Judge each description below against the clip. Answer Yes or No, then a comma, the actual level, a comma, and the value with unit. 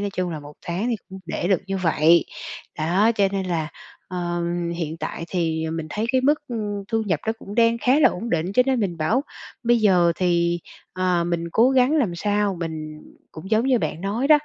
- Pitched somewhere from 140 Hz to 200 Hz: Yes, high, 190 Hz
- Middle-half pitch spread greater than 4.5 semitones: Yes, average, 4.9 semitones